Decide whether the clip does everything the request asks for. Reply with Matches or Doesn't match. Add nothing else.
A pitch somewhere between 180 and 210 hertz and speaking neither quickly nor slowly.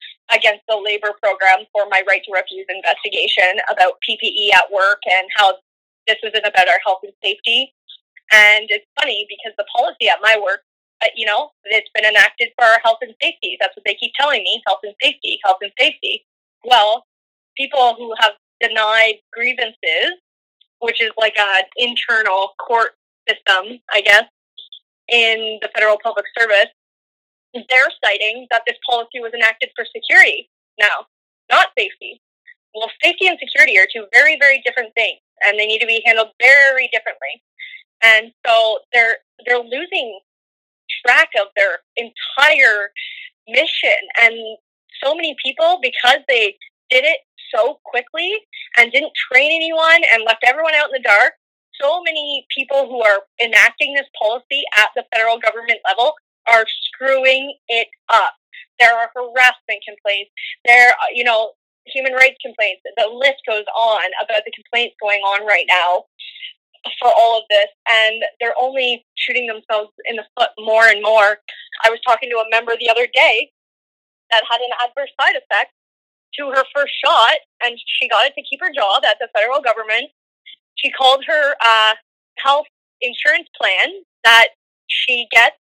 Doesn't match